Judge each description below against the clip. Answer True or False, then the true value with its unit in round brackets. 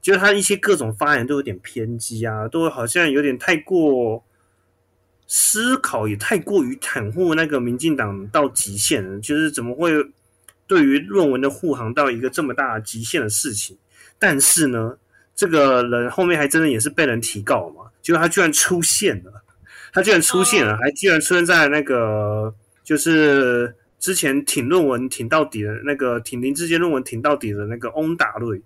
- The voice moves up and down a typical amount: False (6.5 semitones)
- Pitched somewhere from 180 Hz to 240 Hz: False (130 Hz)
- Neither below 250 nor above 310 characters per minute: True (270 characters per minute)